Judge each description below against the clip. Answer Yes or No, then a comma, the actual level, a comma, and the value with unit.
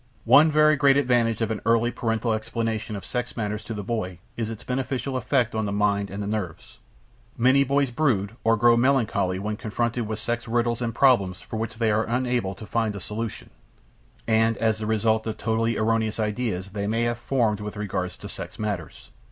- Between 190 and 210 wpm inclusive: Yes, average, 200 wpm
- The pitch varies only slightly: Yes, narrow, 2.2 semitones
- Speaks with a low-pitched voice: Yes, low, 115 Hz